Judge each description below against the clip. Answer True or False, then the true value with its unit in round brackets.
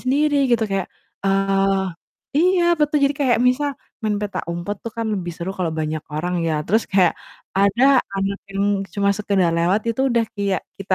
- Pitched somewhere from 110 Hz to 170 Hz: False (200 Hz)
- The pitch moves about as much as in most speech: True (4.1 semitones)